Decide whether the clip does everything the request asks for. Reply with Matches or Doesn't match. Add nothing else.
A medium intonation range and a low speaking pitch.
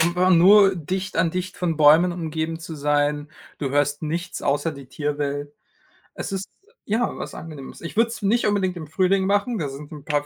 Doesn't match